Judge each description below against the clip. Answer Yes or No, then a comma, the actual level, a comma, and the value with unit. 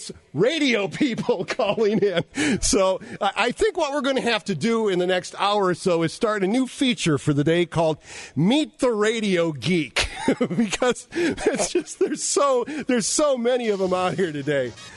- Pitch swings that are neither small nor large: No, wide, 6.1 semitones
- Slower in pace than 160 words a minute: No, average, 185 wpm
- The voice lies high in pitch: Yes, high, 215 Hz